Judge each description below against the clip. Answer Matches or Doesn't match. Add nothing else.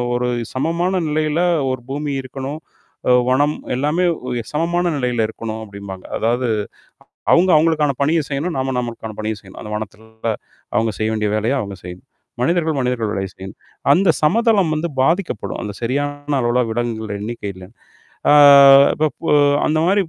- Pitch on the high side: Doesn't match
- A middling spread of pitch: Doesn't match